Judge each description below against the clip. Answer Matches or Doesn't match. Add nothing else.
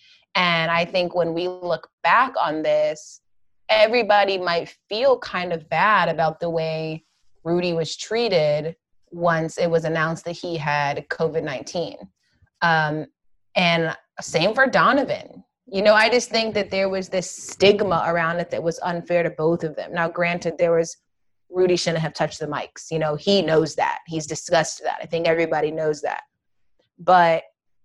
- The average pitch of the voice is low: Doesn't match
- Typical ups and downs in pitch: Doesn't match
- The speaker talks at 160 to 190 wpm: Matches